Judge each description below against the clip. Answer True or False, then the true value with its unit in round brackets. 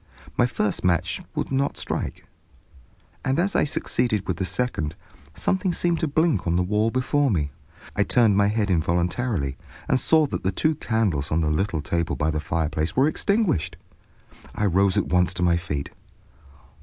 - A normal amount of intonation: False (7.7 semitones)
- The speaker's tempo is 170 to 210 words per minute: True (175 wpm)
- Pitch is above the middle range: False (100 Hz)